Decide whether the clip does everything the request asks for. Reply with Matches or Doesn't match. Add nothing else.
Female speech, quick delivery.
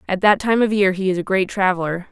Matches